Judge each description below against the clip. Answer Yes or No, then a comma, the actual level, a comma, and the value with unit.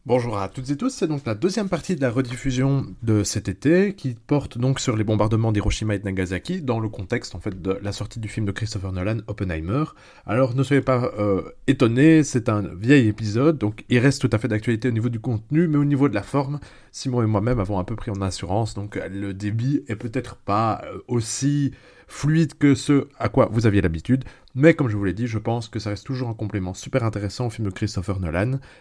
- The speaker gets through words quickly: Yes, fast, 235 wpm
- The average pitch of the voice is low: Yes, low, 115 Hz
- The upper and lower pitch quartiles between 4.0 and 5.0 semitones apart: Yes, average, 4.7 semitones